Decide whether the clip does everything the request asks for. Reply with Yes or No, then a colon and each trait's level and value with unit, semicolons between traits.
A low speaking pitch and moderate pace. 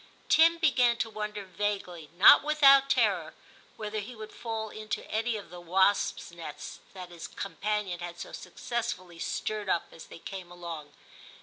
No: high, 205 Hz; average, 160 wpm